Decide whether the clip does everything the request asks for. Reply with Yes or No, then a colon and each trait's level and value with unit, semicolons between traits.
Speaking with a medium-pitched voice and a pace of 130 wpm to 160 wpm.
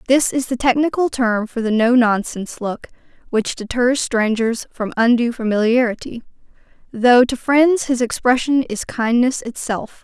No: high, 240 Hz; average, 145 wpm